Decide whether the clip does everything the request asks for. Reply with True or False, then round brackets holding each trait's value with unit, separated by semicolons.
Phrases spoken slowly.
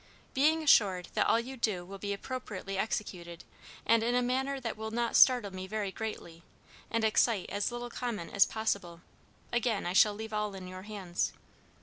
False (185 wpm)